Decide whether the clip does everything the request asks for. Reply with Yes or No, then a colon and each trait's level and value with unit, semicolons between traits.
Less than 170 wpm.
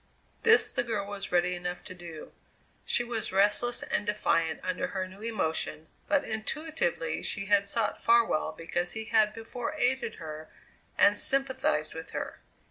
Yes: average, 155 wpm